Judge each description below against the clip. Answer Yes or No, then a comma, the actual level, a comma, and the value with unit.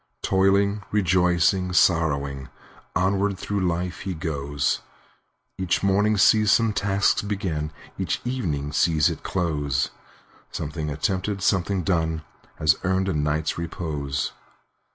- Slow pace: Yes, slow, 105 wpm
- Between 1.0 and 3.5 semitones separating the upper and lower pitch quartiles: No, average, 4.2 semitones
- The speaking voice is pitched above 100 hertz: No, very low, 90 Hz